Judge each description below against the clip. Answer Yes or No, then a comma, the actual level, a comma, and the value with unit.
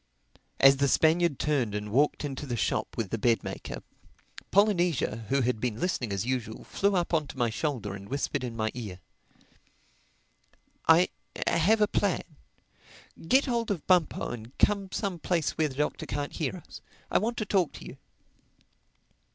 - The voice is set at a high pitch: No, medium, 145 Hz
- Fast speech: No, average, 170 wpm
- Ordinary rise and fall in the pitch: No, wide, 7.2 semitones